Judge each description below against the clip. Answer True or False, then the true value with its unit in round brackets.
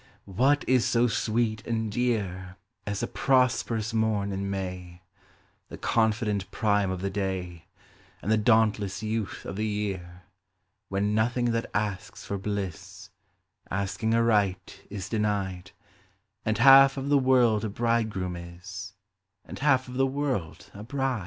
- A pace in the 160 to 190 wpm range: False (140 wpm)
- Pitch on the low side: True (105 Hz)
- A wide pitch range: False (3.3 semitones)